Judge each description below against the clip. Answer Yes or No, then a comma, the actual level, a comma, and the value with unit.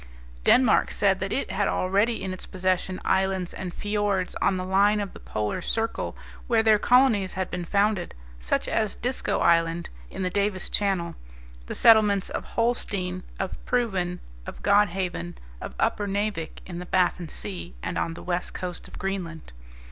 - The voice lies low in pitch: No, high, 190 Hz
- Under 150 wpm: No, average, 165 wpm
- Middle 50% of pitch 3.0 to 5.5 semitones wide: No, narrow, 2.5 semitones